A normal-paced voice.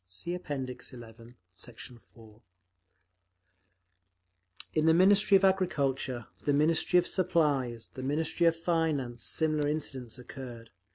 No: slow, 115 wpm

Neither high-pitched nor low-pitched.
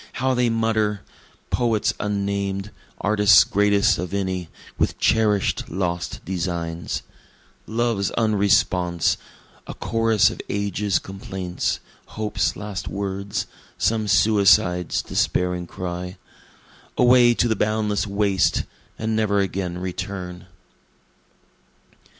No: low, 100 Hz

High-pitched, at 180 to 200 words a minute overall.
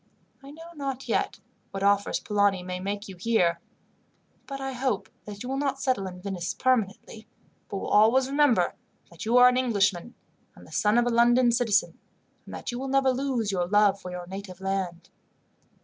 Yes: high, 215 Hz; average, 190 wpm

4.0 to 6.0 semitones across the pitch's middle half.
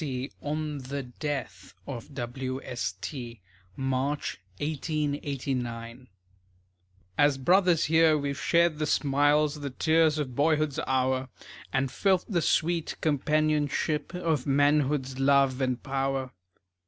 No: average, 2.7 semitones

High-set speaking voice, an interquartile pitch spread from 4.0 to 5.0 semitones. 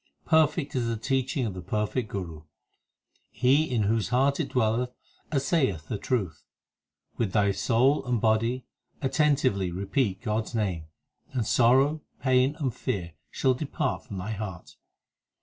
No: low, 120 Hz; average, 4.7 semitones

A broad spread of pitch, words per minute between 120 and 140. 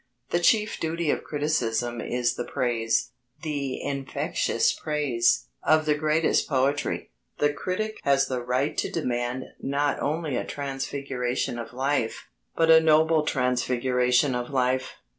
No: average, 3.5 semitones; slow, 135 wpm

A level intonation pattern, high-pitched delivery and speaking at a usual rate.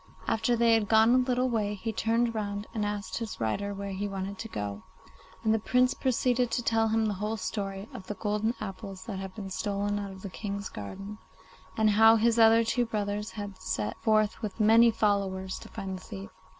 No: narrow, 2.3 semitones; high, 210 Hz; fast, 215 wpm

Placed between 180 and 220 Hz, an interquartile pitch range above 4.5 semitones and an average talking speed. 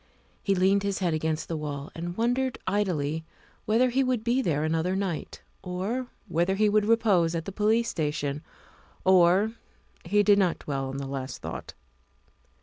Yes: medium, 185 Hz; average, 5.1 semitones; average, 165 wpm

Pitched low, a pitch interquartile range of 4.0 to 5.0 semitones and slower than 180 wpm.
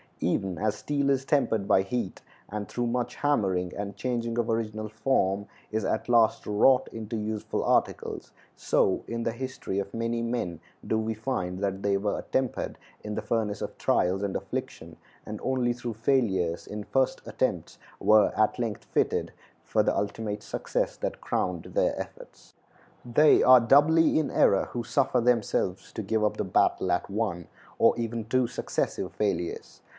No: low, 110 Hz; average, 3.2 semitones; average, 165 wpm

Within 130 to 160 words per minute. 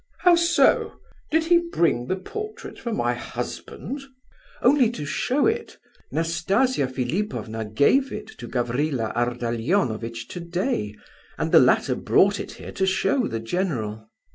Yes: average, 140 wpm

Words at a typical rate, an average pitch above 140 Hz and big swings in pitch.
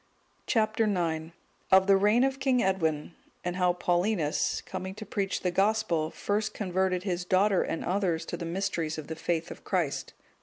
No: average, 175 wpm; medium, 185 Hz; average, 3.3 semitones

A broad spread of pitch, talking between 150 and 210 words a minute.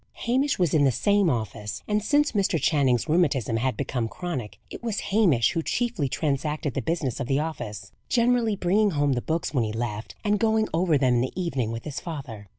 Yes: wide, 8.3 semitones; fast, 205 wpm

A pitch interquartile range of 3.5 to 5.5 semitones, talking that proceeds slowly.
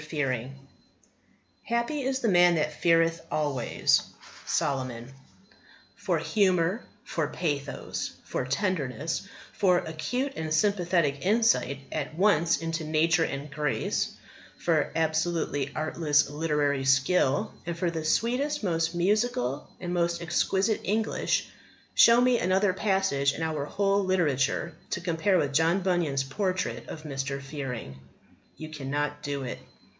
Yes: average, 4.6 semitones; slow, 125 wpm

